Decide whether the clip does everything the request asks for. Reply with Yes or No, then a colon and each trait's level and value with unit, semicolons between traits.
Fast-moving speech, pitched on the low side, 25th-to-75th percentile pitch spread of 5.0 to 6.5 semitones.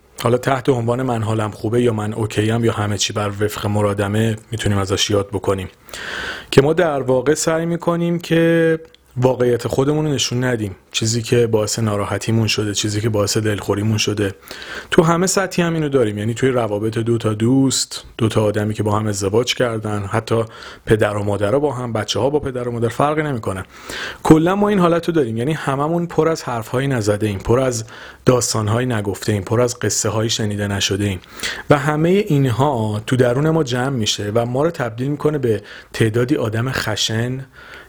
No: fast, 185 wpm; low, 115 Hz; average, 4.5 semitones